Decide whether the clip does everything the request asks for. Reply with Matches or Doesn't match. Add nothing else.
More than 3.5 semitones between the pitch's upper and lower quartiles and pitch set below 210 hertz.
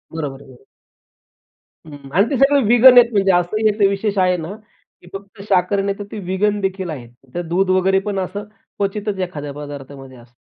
Matches